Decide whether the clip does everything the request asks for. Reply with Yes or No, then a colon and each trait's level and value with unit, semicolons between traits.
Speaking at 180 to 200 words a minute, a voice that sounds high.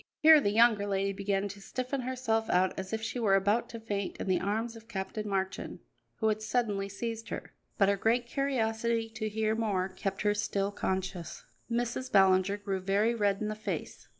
Yes: average, 195 wpm; high, 210 Hz